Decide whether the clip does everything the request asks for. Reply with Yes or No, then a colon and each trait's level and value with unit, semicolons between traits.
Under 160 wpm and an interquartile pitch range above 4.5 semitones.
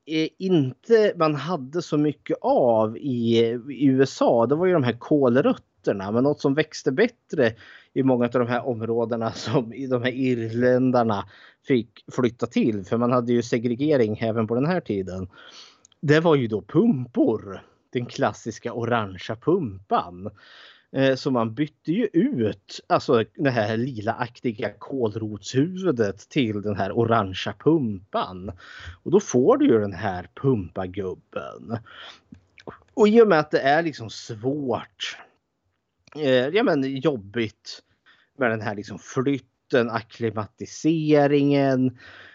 No: average, 135 wpm; average, 4.1 semitones